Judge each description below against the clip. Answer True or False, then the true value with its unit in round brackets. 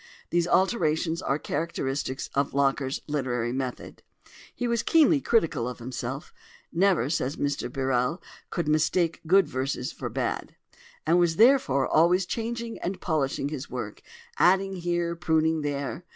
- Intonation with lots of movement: False (4.8 semitones)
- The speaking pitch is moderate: True (160 Hz)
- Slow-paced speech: True (130 wpm)